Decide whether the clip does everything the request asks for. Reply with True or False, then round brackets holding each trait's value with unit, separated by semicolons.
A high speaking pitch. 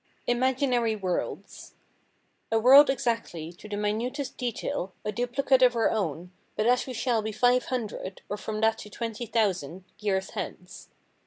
True (225 Hz)